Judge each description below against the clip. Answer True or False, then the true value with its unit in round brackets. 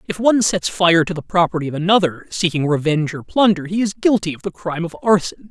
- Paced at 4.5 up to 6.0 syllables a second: False (6.2 syllables/s)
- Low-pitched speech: False (175 Hz)